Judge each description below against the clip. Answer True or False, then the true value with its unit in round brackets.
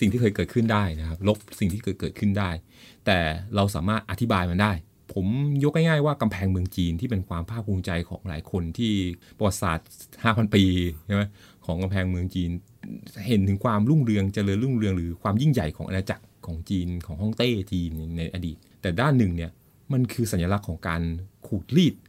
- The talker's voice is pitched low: True (100 Hz)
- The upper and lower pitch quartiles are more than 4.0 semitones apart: False (3.7 semitones)